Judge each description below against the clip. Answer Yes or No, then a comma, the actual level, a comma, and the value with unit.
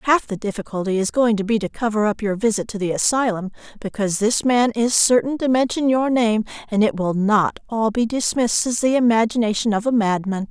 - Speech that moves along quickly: Yes, fast, 210 wpm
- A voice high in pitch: Yes, high, 220 Hz